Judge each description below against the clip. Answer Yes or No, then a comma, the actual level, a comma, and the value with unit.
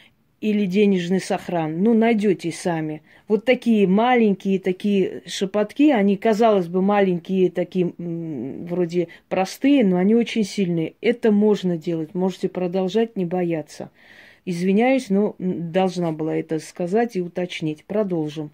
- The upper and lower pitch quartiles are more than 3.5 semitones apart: No, average, 3.2 semitones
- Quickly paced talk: No, average, 125 wpm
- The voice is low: No, high, 190 Hz